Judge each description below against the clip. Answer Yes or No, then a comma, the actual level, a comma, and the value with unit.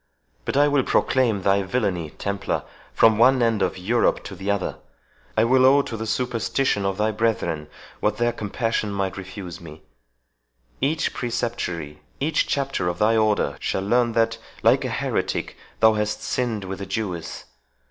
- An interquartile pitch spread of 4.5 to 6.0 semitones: No, average, 3.6 semitones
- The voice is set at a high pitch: No, low, 110 Hz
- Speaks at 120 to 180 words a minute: Yes, average, 160 wpm